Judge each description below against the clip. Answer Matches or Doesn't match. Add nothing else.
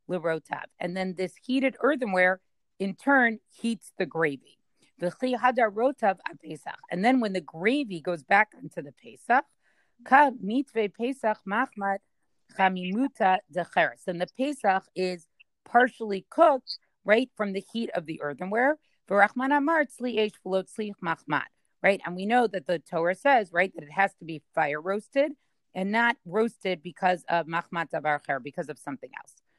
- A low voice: Doesn't match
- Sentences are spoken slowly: Matches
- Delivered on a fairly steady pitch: Doesn't match